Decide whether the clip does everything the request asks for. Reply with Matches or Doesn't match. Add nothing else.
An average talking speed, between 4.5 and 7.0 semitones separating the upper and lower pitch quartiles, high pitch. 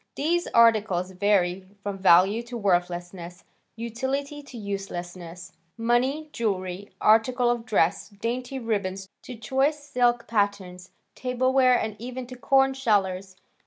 Doesn't match